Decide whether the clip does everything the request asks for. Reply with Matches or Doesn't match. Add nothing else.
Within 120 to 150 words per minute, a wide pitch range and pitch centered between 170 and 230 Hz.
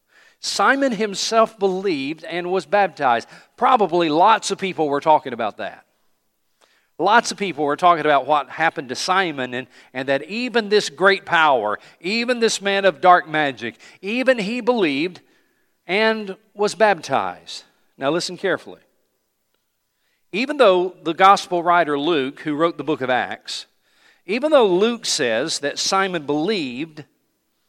Matches